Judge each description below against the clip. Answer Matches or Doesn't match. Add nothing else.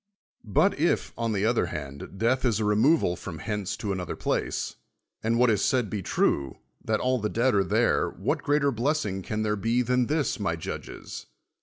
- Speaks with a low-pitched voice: Matches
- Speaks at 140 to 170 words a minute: Doesn't match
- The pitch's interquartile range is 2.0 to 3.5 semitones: Doesn't match